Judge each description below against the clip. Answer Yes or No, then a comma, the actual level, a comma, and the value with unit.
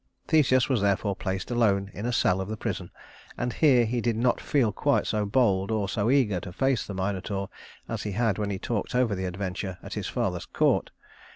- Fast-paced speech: Yes, fast, 210 wpm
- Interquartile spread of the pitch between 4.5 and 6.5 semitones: No, average, 3.8 semitones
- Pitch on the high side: No, low, 105 Hz